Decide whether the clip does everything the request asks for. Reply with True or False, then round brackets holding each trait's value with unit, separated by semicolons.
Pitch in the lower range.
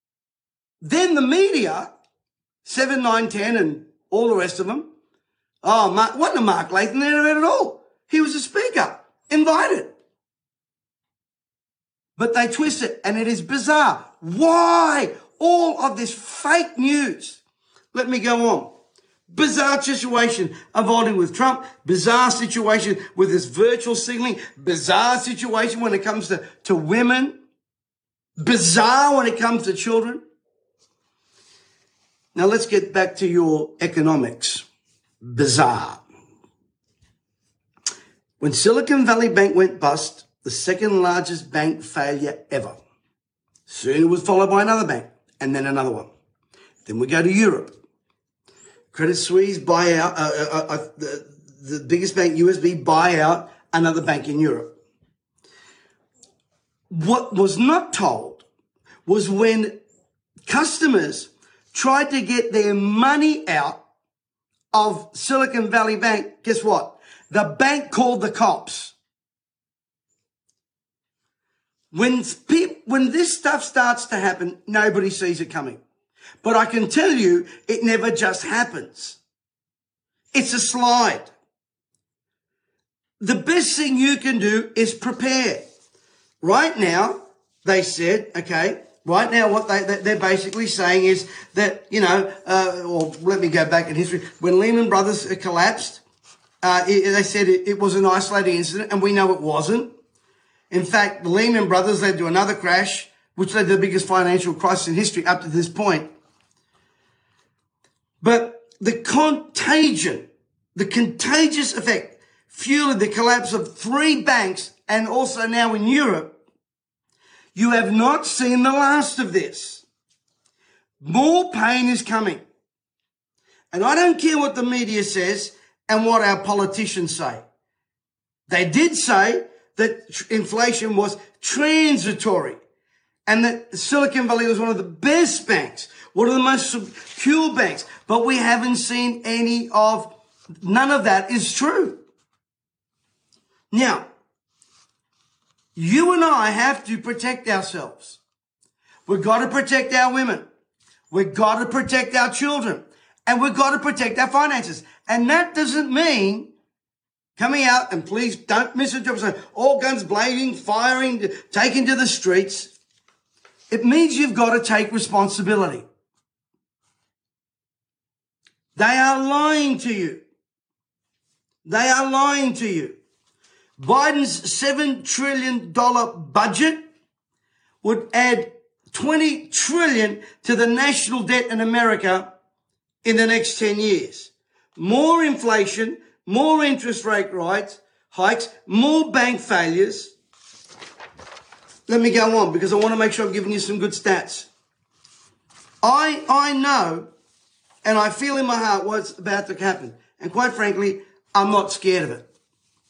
False (225 Hz)